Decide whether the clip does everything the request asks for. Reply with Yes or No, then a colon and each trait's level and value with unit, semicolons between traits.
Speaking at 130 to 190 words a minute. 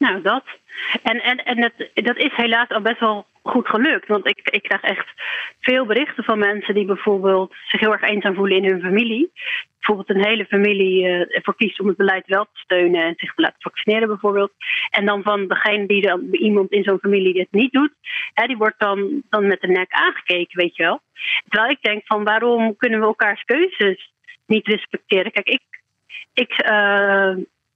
No: fast, 200 wpm